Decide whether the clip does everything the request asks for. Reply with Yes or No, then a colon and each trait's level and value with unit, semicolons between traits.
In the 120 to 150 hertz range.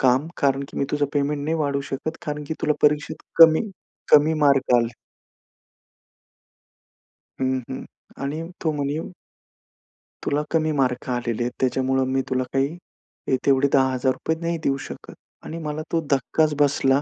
Yes: medium, 140 Hz